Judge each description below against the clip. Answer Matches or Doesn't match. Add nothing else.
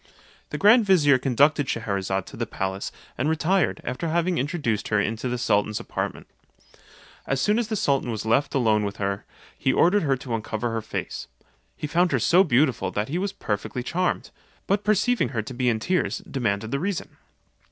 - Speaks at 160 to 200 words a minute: Matches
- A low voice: Matches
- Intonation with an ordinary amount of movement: Doesn't match